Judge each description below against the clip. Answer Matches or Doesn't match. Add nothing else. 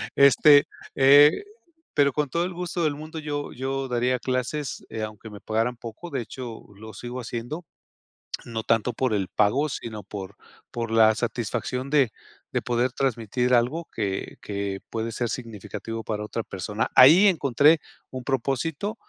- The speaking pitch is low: Matches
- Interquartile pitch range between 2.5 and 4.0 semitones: Doesn't match